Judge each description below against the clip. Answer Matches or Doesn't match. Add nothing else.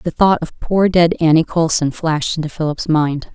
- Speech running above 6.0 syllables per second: Doesn't match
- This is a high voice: Doesn't match